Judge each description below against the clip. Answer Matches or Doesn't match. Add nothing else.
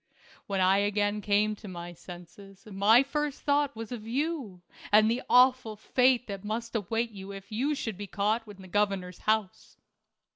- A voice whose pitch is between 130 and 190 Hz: Doesn't match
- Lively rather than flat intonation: Doesn't match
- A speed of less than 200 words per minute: Matches